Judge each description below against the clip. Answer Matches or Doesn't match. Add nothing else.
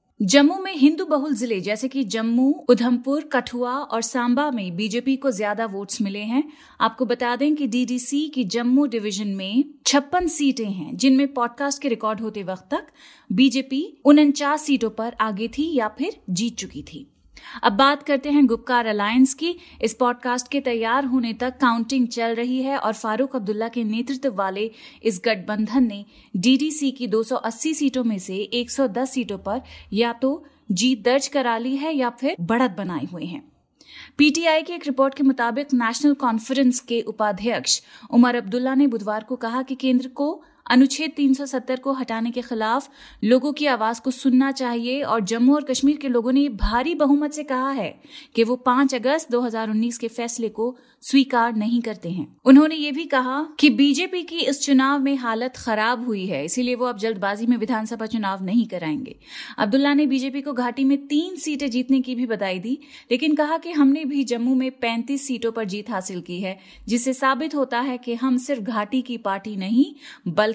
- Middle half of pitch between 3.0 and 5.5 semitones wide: Matches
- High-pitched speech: Matches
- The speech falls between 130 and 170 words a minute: Doesn't match